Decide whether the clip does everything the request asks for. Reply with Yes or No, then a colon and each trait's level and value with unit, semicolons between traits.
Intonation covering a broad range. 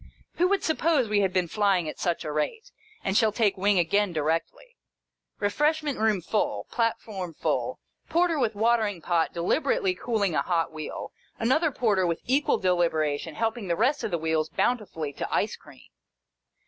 Yes: wide, 6.4 semitones